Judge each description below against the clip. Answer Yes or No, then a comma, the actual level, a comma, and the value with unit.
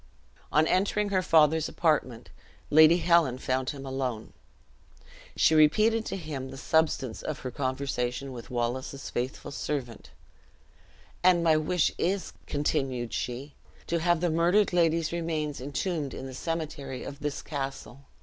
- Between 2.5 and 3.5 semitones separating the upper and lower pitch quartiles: No, average, 4.1 semitones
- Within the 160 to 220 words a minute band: No, average, 140 wpm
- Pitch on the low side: No, medium, 150 Hz